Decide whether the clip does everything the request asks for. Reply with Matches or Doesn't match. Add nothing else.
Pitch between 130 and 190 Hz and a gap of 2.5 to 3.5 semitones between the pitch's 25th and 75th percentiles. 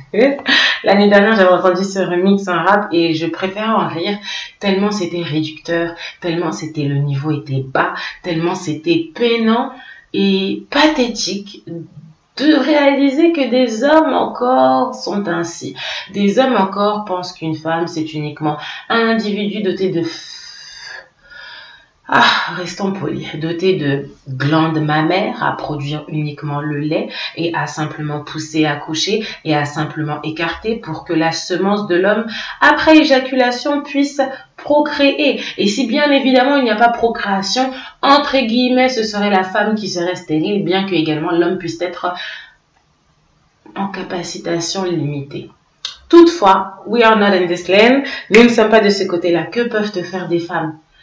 Doesn't match